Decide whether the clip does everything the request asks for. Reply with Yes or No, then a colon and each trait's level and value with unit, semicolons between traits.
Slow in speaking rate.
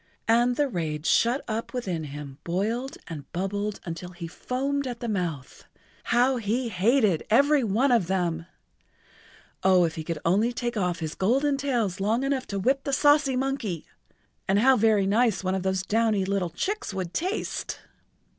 No: average, 170 wpm